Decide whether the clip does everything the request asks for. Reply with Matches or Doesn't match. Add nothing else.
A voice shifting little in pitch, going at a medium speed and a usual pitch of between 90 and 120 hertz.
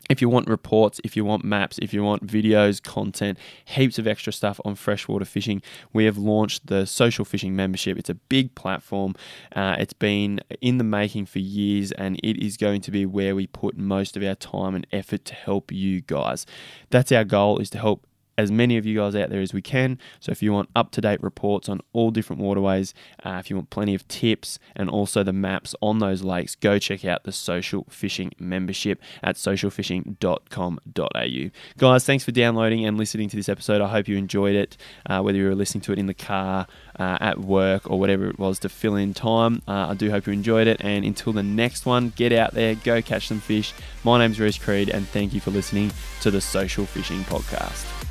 Doesn't match